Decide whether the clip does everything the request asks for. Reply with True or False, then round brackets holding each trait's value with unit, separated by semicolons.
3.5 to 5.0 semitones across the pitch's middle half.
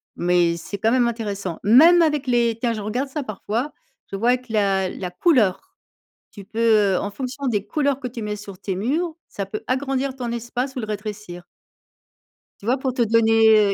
True (4.1 semitones)